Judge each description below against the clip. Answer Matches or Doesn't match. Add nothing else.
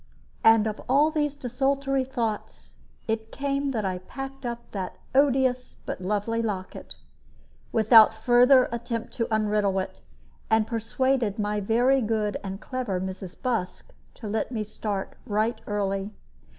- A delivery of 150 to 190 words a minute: Doesn't match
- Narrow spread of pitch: Doesn't match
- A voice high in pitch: Matches